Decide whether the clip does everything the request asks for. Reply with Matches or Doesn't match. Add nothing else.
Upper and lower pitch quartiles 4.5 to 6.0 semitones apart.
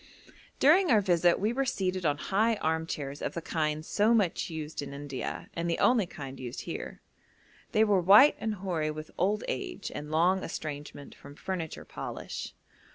Matches